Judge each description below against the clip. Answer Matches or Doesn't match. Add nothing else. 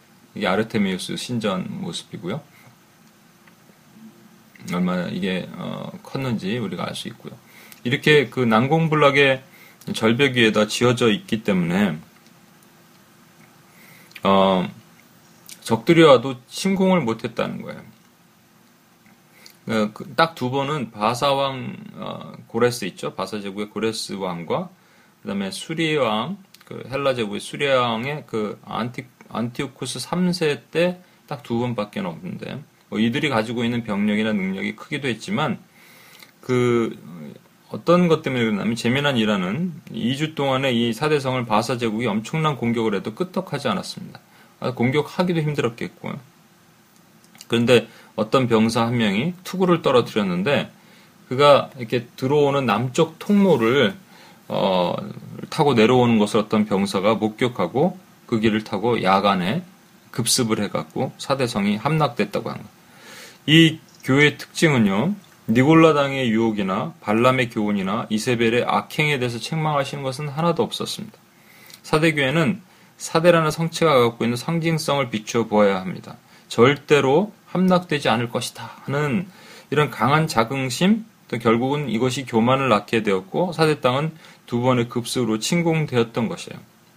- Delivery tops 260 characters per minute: Matches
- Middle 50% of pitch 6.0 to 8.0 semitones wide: Matches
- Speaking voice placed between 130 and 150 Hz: Matches